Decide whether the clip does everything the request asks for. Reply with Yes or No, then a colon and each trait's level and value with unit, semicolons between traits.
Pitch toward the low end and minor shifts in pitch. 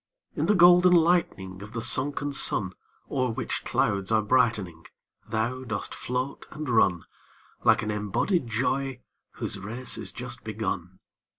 No: low, 115 Hz; average, 4.6 semitones